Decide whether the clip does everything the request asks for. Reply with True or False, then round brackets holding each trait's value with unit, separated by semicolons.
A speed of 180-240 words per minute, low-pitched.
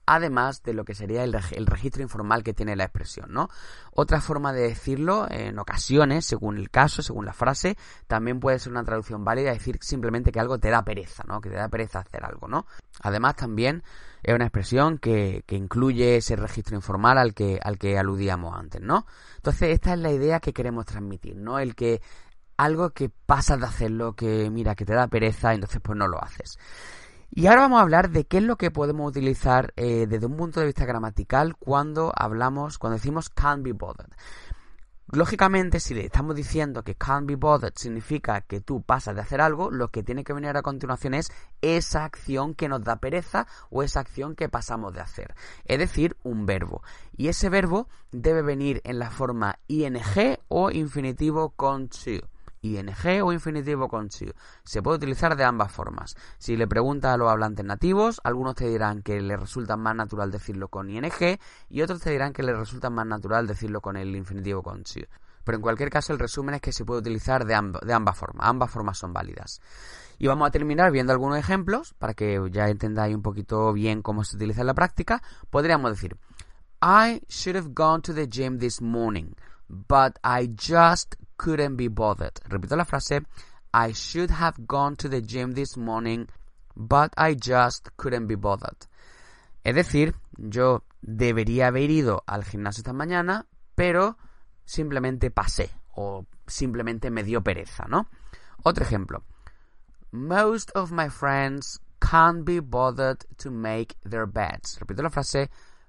True (185 wpm; 120 Hz)